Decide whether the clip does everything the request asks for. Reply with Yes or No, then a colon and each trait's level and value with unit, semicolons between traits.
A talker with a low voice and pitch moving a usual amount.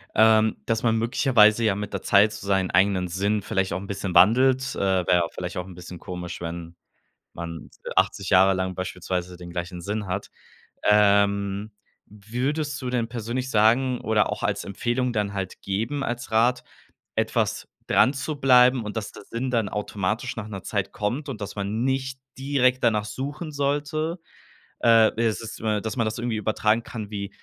Yes: low, 105 Hz; average, 3.9 semitones